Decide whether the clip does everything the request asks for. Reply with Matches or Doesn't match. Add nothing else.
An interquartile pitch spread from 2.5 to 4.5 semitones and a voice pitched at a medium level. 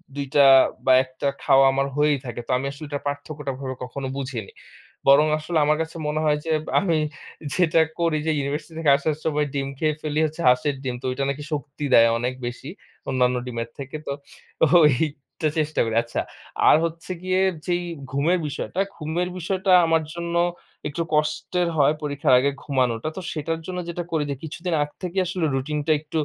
Matches